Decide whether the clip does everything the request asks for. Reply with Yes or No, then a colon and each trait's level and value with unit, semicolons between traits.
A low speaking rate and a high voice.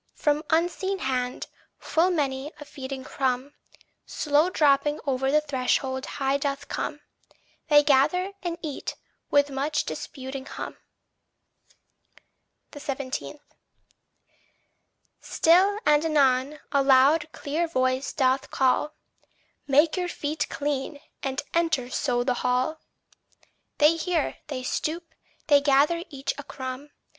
Yes: slow, 115 wpm; very high, 285 Hz